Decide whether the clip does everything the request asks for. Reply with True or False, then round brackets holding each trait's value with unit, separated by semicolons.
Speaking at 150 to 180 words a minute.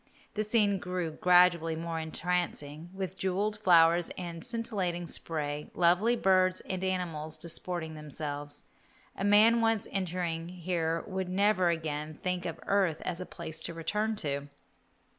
False (140 wpm)